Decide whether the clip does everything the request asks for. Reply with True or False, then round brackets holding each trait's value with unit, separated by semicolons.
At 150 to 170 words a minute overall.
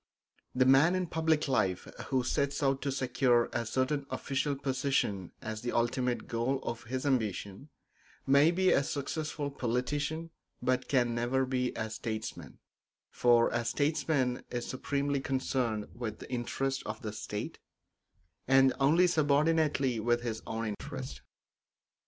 False (140 wpm)